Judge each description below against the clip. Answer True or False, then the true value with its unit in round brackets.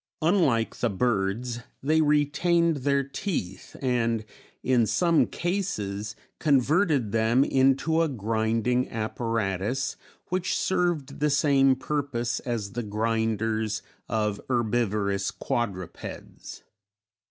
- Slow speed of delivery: True (95 wpm)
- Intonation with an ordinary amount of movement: True (4.7 semitones)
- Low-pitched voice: True (120 Hz)